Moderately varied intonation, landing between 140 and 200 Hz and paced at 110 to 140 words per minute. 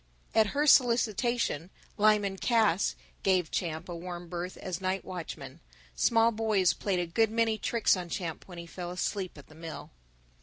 No: average, 4.2 semitones; high, 190 Hz; average, 165 wpm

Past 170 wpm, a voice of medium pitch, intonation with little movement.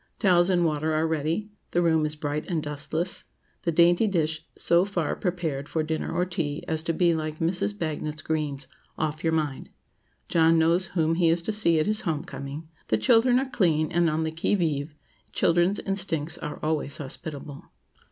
Yes: average, 180 wpm; medium, 160 Hz; narrow, 2.2 semitones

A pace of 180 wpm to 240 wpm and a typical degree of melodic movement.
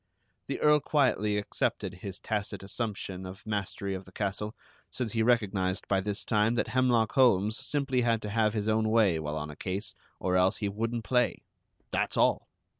Yes: average, 185 wpm; average, 3.1 semitones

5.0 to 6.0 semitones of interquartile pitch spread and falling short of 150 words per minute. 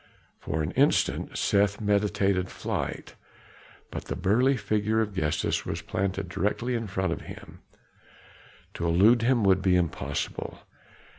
No: average, 3.1 semitones; slow, 135 wpm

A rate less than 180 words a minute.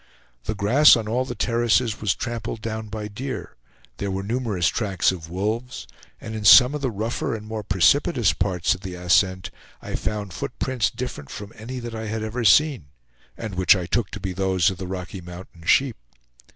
No: average, 195 wpm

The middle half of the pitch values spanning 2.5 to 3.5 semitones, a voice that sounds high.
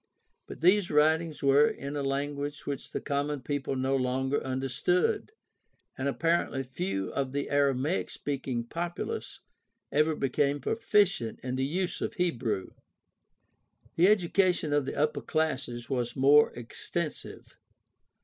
No: average, 3.2 semitones; medium, 140 Hz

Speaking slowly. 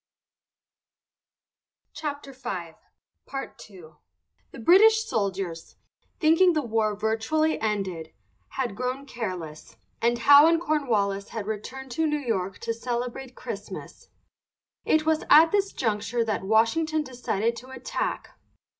Yes: slow, 115 wpm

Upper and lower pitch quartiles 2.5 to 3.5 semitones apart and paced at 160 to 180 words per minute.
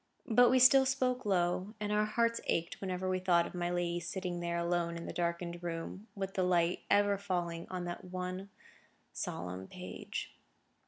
Yes: average, 2.8 semitones; average, 175 wpm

